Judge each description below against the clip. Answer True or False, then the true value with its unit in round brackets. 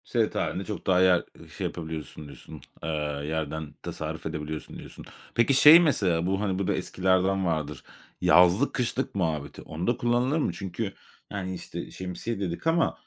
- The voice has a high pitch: False (95 Hz)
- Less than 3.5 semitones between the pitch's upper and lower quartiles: False (4.8 semitones)